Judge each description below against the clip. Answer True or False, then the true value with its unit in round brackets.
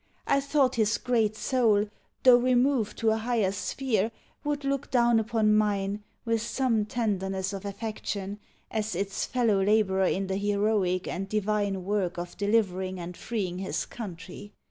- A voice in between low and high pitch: False (210 Hz)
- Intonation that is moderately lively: True (3.0 semitones)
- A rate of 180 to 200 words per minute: False (150 wpm)